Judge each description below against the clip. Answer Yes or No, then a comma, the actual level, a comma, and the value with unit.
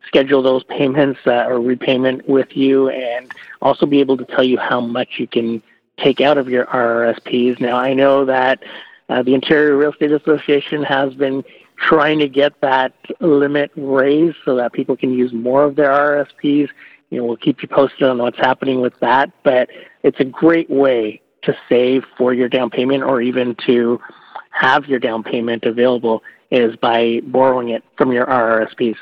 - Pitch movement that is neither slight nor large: No, narrow, 2.3 semitones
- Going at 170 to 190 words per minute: Yes, average, 180 wpm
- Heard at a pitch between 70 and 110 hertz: No, low, 130 Hz